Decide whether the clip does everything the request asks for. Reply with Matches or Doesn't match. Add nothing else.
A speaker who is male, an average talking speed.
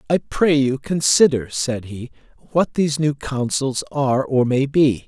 Matches